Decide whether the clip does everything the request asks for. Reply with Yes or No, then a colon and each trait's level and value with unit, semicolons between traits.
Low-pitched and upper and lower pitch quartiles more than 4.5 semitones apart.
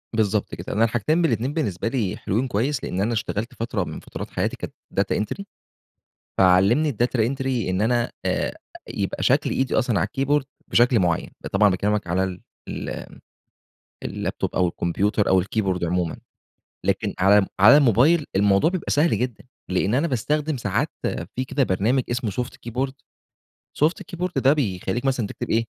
Yes: low, 115 Hz; average, 5.3 semitones